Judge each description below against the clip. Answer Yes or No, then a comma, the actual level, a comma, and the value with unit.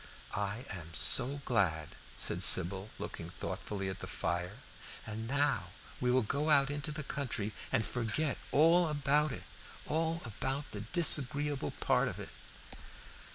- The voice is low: Yes, low, 130 Hz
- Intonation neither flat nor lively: No, wide, 6.0 semitones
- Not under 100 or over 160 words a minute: Yes, average, 145 wpm